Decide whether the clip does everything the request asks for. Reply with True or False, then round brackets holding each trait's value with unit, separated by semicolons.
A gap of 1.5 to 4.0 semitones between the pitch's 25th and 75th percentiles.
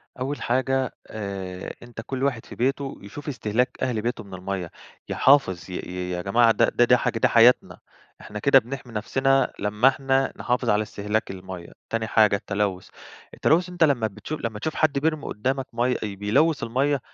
False (4.4 semitones)